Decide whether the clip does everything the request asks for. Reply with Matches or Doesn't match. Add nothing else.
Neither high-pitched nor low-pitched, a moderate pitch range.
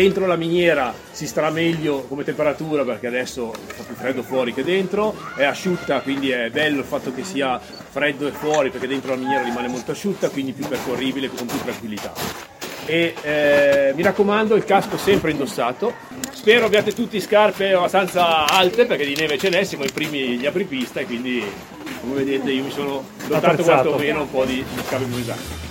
Doesn't match